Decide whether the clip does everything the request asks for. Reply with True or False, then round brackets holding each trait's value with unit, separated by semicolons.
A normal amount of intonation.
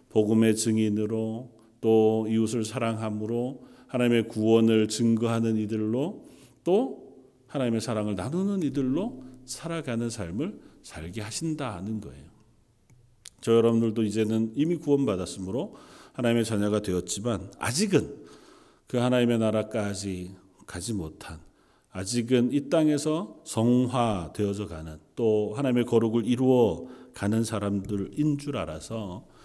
True (3.0 semitones)